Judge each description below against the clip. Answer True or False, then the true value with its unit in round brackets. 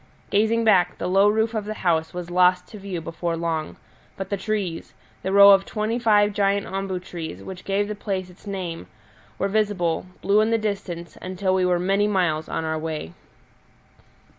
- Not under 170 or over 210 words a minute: True (190 wpm)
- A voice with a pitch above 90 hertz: True (190 Hz)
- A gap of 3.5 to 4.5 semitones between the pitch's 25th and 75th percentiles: False (2.9 semitones)